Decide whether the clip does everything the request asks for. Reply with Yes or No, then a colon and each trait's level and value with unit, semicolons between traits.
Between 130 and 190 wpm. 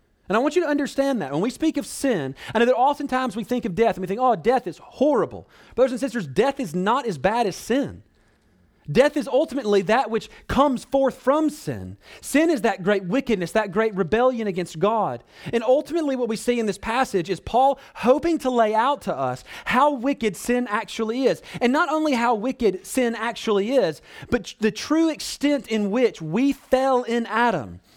No: fast, 205 wpm